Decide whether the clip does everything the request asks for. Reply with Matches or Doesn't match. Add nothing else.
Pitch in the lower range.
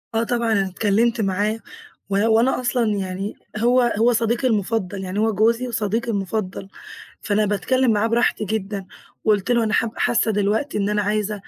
Doesn't match